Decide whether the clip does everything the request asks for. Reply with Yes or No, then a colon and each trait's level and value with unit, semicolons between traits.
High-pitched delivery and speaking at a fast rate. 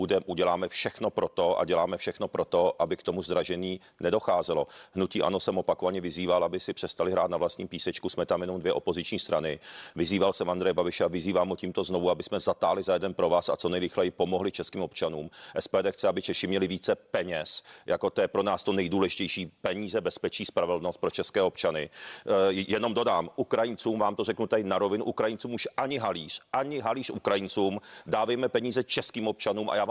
No: low, 125 Hz; fast, 195 wpm